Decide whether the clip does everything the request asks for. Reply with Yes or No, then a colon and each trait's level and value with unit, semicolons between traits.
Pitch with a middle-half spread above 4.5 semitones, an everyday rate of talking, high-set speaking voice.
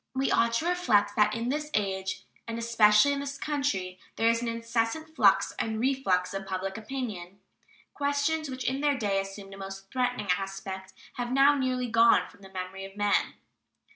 Yes: wide, 5.4 semitones; average, 180 wpm; high, 230 Hz